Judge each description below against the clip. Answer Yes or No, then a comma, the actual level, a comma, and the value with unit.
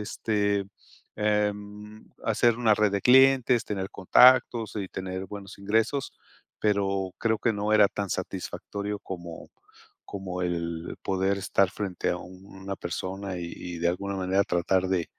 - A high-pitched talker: No, low, 100 Hz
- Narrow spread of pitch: Yes, narrow, 2.1 semitones